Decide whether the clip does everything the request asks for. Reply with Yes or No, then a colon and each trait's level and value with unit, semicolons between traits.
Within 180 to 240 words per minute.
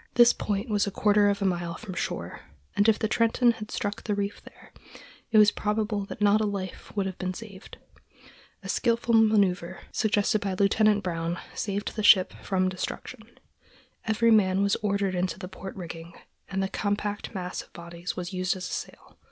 Yes: average, 190 wpm